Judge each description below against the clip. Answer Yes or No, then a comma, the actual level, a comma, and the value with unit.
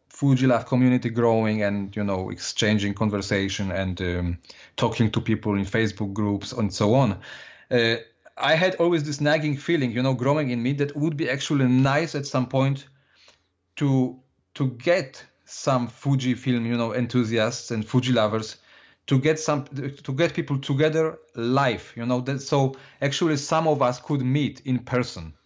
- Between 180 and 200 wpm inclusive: No, average, 170 wpm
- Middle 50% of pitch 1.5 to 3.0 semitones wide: No, average, 4.0 semitones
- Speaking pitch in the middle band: No, low, 130 Hz